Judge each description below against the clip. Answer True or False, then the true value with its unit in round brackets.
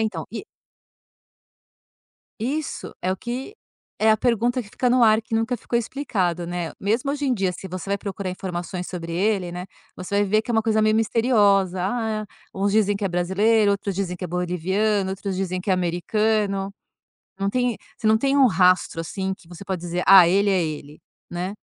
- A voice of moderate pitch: False (200 Hz)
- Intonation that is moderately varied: True (3.4 semitones)